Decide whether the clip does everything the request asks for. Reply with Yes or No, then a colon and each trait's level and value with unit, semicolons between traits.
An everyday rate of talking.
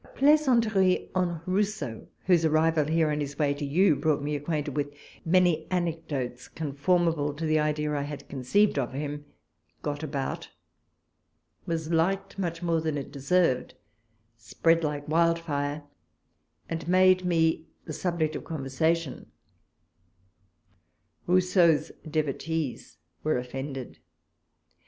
No: slow, 130 wpm